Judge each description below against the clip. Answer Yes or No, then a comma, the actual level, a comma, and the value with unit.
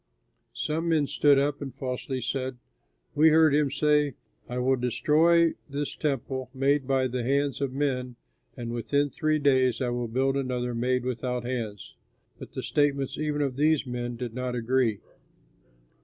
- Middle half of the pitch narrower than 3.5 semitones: Yes, average, 2.7 semitones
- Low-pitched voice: Yes, low, 130 Hz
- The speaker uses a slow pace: No, average, 160 wpm